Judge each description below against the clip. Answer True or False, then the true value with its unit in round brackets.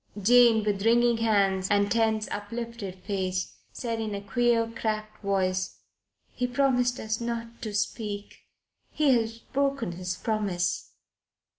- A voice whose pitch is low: False (220 Hz)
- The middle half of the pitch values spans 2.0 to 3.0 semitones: True (2.7 semitones)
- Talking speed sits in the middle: False (130 wpm)